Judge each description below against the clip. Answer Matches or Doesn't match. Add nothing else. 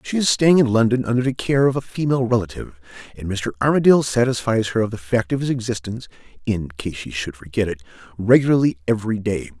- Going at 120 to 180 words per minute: Doesn't match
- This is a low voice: Matches